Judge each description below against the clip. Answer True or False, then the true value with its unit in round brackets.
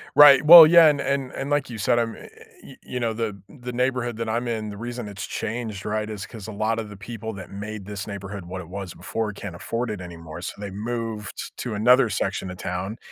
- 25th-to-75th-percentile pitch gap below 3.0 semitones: False (3.5 semitones)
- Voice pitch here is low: True (110 Hz)